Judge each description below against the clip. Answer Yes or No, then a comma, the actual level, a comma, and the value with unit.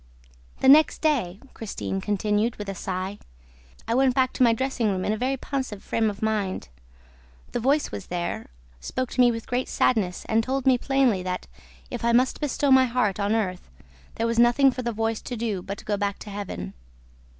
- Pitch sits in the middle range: No, high, 225 Hz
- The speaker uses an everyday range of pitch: Yes, average, 4.2 semitones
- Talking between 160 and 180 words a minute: No, fast, 205 wpm